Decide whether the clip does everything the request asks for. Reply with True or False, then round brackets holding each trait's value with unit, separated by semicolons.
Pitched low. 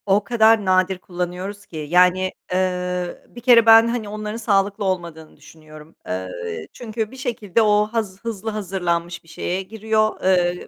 False (190 Hz)